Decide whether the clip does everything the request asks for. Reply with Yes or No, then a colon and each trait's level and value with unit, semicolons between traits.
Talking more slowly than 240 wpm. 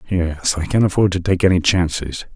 Yes: fast, 205 wpm